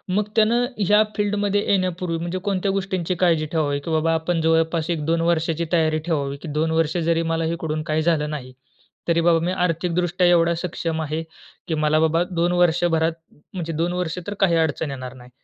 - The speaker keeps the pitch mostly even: Yes, narrow, 1.9 semitones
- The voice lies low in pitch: No, medium, 165 Hz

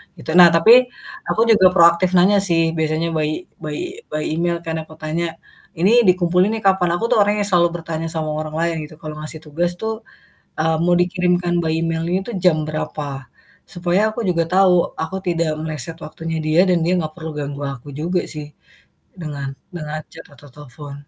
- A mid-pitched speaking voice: Yes, medium, 165 Hz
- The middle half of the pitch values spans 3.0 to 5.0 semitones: No, narrow, 2.5 semitones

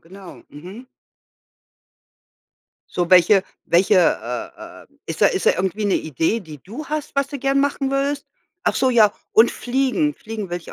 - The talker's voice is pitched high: Yes, high, 215 Hz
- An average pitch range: No, wide, 7.4 semitones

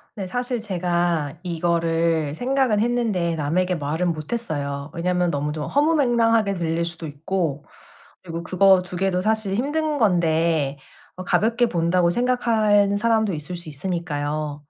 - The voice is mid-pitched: Yes, medium, 180 Hz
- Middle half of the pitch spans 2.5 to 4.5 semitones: No, average, 5.1 semitones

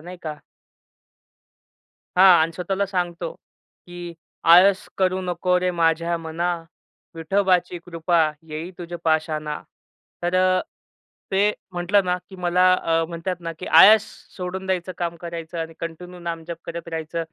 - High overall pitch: No, medium, 175 Hz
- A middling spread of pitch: No, narrow, 1.6 semitones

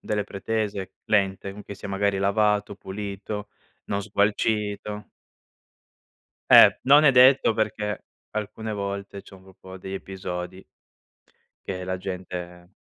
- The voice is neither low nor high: No, low, 100 Hz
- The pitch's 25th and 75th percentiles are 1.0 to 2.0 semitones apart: Yes, narrow, 1.7 semitones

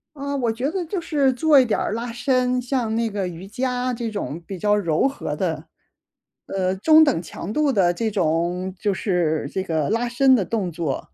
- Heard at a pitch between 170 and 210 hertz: No, high, 225 Hz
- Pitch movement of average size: No, wide, 5.8 semitones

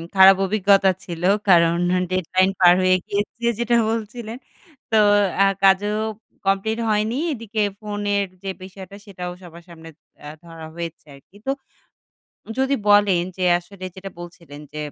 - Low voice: No, high, 195 Hz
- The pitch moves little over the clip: No, average, 3.1 semitones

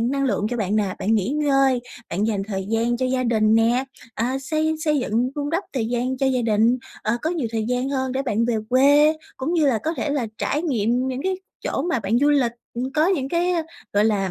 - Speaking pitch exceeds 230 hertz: Yes, very high, 255 Hz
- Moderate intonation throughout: Yes, average, 4.2 semitones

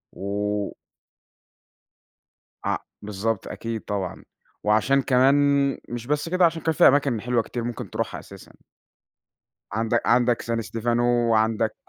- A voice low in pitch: Yes, low, 115 Hz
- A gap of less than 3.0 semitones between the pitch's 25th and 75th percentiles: Yes, narrow, 2.5 semitones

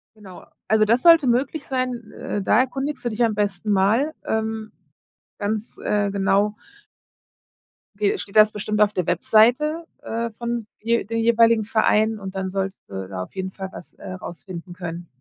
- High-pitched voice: Yes, high, 215 Hz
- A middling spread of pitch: Yes, average, 3.2 semitones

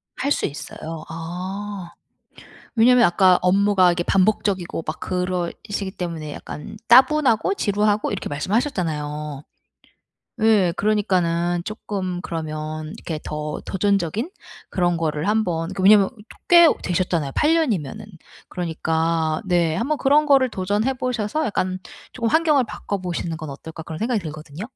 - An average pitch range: Yes, average, 4.6 semitones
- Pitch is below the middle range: No, medium, 185 Hz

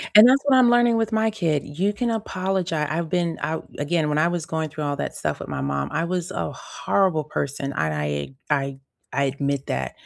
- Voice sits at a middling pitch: Yes, medium, 160 Hz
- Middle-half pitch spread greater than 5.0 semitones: Yes, wide, 5.6 semitones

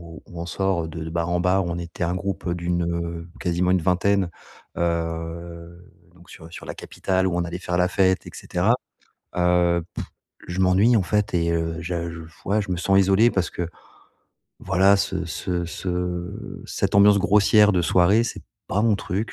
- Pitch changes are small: Yes, narrow, 2.1 semitones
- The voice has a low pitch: Yes, very low, 90 Hz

